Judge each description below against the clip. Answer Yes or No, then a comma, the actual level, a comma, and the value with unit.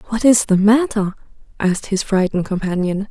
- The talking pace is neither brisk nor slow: Yes, average, 155 wpm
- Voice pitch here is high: Yes, high, 205 Hz